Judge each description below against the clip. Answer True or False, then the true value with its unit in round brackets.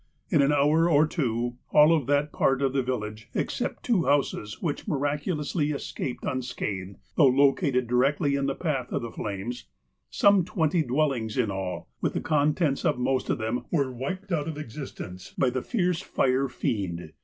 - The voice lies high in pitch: False (140 Hz)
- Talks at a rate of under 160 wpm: False (175 wpm)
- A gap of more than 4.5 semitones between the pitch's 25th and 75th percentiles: False (3.8 semitones)